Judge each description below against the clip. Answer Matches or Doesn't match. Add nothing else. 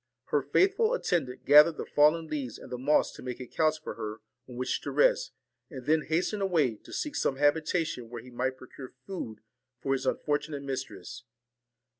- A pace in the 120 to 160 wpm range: Doesn't match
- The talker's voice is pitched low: Doesn't match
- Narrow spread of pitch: Doesn't match